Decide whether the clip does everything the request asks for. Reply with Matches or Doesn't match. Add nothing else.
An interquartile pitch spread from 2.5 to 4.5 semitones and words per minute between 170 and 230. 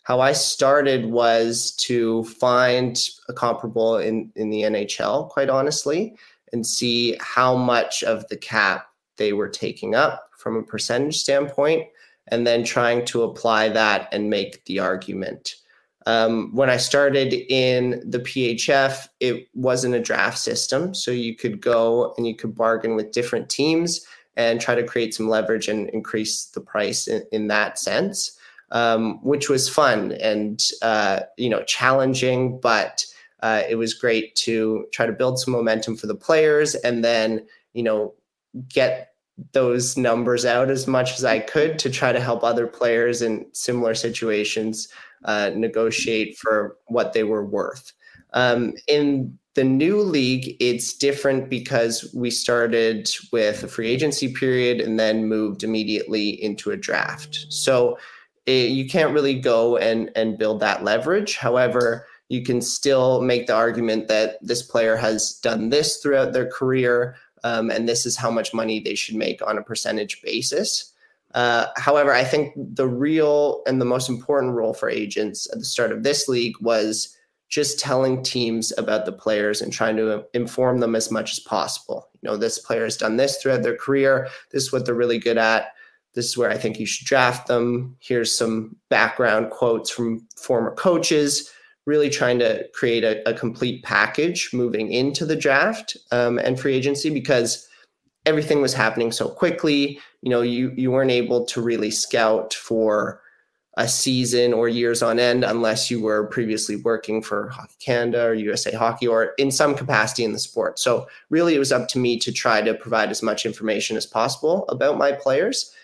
Matches